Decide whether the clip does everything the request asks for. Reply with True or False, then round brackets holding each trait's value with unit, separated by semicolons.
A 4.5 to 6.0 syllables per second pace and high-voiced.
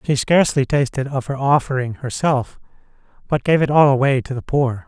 False (5.5 syllables/s; 135 Hz)